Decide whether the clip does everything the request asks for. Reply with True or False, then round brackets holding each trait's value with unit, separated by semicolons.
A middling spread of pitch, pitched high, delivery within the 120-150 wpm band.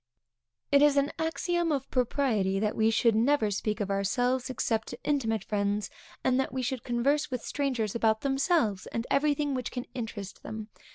False (4.4 semitones; 245 Hz; 180 wpm)